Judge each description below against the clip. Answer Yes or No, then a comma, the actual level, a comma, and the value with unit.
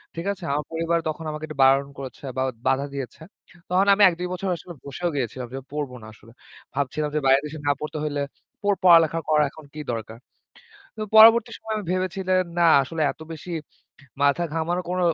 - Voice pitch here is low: No, medium, 155 Hz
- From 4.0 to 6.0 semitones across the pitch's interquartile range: Yes, average, 4.3 semitones